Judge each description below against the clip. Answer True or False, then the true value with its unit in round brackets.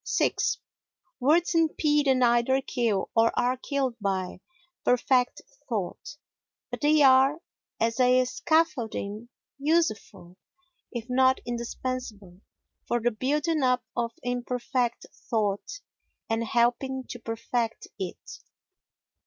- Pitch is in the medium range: False (245 Hz)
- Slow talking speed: True (105 wpm)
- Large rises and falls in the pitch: False (2.8 semitones)